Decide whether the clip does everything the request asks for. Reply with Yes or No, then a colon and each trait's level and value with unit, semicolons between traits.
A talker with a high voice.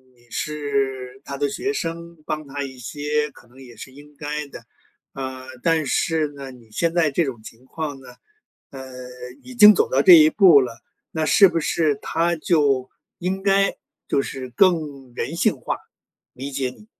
No: medium, 145 Hz